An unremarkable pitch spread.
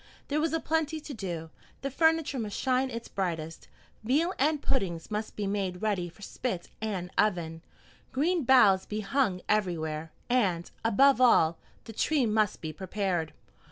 No: wide, 6.9 semitones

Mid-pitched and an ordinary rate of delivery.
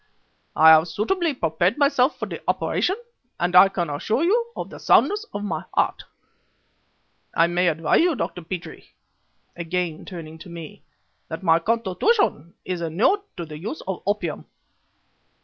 Yes: medium, 180 Hz; average, 150 wpm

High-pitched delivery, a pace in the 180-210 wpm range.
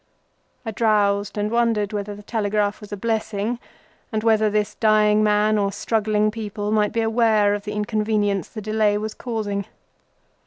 No: high, 210 Hz; average, 155 wpm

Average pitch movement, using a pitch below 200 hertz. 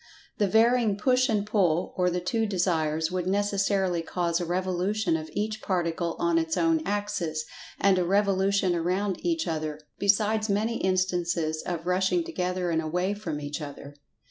Yes: average, 3.3 semitones; medium, 185 Hz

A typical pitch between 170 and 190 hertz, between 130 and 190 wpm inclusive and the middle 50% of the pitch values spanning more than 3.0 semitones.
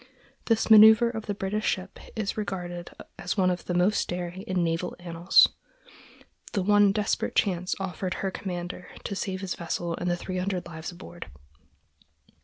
No: medium, 185 Hz; average, 160 wpm; narrow, 2.5 semitones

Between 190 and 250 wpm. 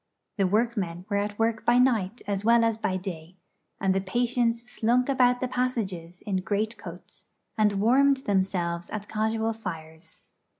No: average, 155 wpm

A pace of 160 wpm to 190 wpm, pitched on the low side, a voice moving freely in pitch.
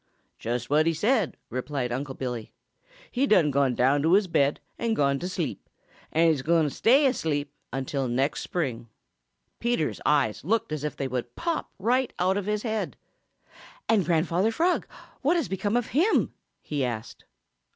No: average, 170 wpm; medium, 160 Hz; wide, 7.9 semitones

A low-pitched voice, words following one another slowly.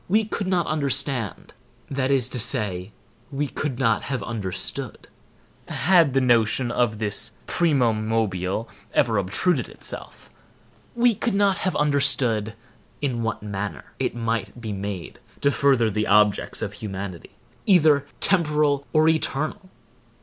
Yes: low, 125 Hz; slow, 130 wpm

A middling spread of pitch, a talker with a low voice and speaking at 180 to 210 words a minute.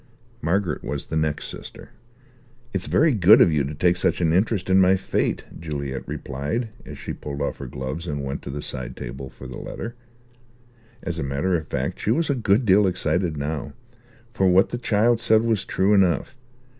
No: wide, 6.0 semitones; very low, 85 Hz; average, 195 wpm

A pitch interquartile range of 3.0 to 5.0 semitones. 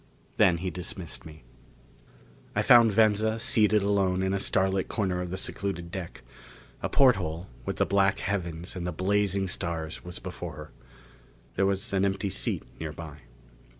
No: narrow, 2.6 semitones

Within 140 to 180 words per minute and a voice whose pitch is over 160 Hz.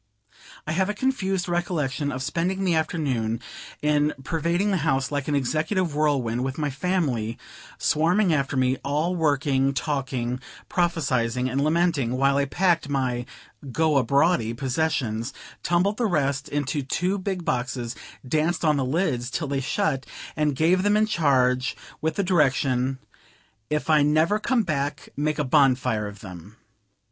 No: average, 150 wpm; medium, 145 Hz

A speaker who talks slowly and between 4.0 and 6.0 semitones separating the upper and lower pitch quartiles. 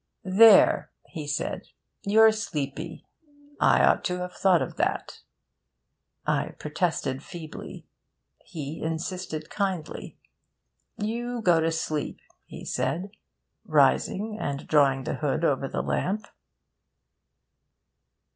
Yes: slow, 105 wpm; average, 4.6 semitones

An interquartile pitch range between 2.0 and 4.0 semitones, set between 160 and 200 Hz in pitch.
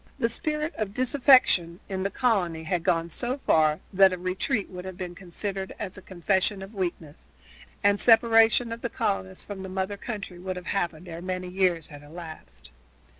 Yes: average, 3.3 semitones; high, 190 Hz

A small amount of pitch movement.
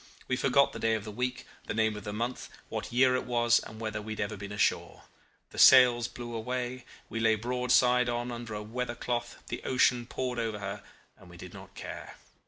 Yes: narrow, 2.3 semitones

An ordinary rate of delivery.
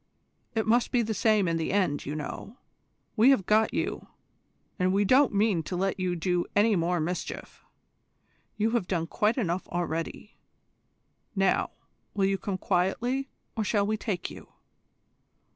Yes: average, 160 wpm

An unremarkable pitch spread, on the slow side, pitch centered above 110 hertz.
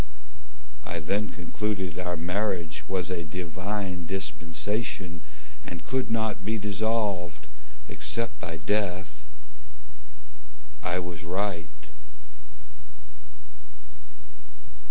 No: average, 3.3 semitones; slow, 80 wpm; very low, 90 Hz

